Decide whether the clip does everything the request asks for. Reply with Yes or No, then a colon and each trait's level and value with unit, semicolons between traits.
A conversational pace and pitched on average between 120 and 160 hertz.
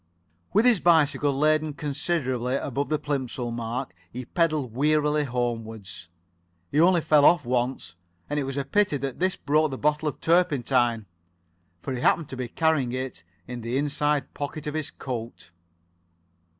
Yes: average, 160 wpm; medium, 140 Hz